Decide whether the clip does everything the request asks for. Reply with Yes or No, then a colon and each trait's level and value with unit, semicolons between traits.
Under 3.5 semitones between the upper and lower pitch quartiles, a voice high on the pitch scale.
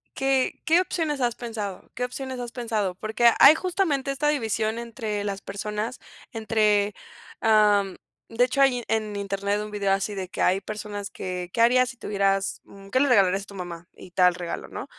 No: average, 4.0 semitones; high, 215 Hz